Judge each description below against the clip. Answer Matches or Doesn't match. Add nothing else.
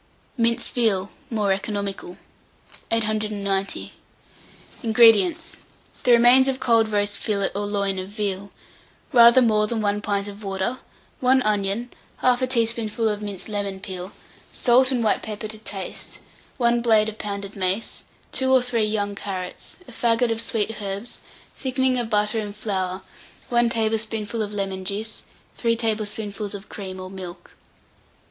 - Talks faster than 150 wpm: Doesn't match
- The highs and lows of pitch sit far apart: Doesn't match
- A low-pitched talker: Doesn't match